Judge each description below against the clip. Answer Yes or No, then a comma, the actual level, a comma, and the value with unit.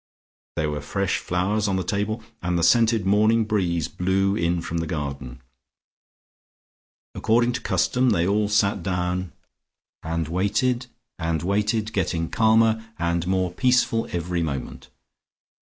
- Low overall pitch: Yes, very low, 95 Hz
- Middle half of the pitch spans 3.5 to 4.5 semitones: Yes, average, 4.2 semitones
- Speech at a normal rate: No, slow, 125 wpm